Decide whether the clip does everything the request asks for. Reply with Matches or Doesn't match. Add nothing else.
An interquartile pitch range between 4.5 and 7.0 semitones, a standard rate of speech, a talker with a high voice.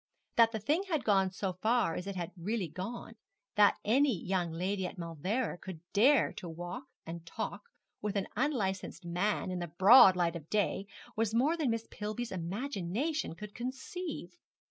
Matches